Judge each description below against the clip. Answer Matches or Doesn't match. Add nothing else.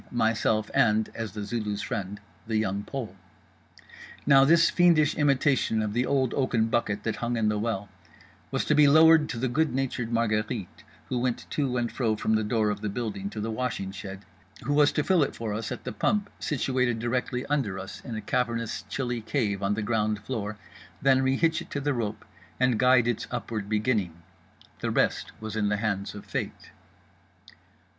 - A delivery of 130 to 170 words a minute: Doesn't match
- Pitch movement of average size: Matches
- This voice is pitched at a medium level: Doesn't match